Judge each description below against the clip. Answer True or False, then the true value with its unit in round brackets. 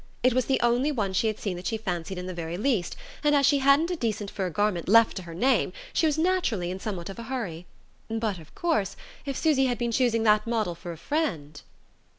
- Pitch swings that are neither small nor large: False (6.4 semitones)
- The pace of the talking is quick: True (235 wpm)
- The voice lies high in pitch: True (220 Hz)